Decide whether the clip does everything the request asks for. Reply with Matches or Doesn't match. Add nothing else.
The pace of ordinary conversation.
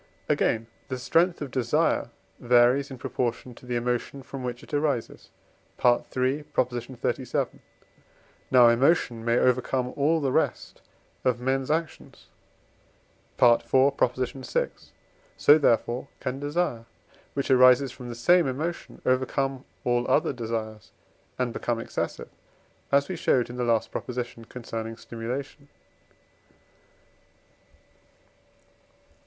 Doesn't match